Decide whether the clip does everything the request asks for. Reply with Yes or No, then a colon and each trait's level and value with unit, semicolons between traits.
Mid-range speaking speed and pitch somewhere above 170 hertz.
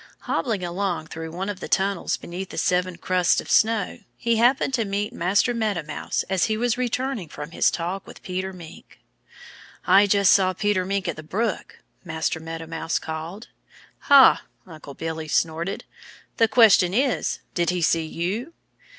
Yes: average, 165 wpm; medium, 185 Hz